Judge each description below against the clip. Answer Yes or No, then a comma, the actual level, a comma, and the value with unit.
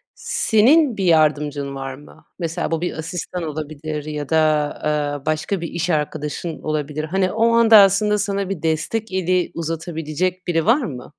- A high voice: No, medium, 165 Hz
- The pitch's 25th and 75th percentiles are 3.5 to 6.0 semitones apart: Yes, average, 4.0 semitones